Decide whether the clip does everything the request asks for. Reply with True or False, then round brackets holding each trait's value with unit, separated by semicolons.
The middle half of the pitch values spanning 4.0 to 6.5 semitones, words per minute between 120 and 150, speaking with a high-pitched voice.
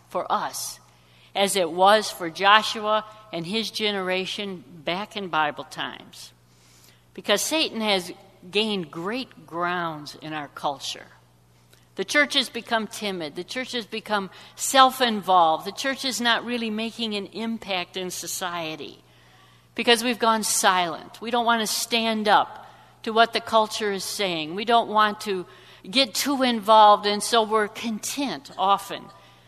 True (4.5 semitones; 145 wpm; 210 Hz)